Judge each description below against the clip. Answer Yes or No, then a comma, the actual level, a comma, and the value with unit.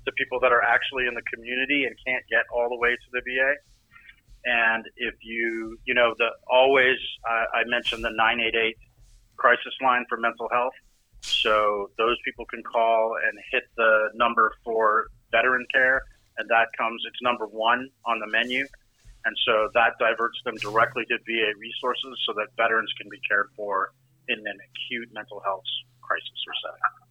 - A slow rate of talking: No, average, 180 wpm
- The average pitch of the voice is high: No, low, 115 Hz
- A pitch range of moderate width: No, narrow, 1.7 semitones